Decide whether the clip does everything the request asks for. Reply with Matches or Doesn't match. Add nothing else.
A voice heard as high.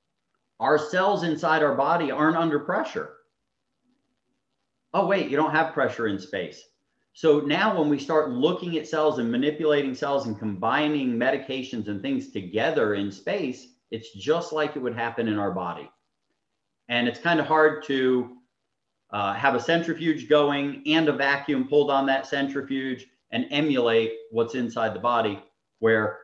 Doesn't match